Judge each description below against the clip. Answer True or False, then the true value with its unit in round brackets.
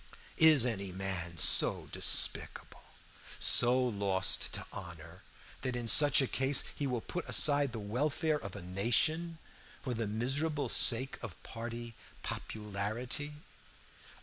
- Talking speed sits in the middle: False (125 wpm)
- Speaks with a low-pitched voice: True (120 Hz)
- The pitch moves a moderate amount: False (5.7 semitones)